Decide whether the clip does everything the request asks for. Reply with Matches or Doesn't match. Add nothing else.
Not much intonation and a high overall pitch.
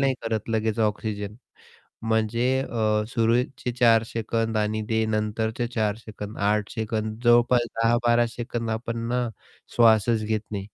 Doesn't match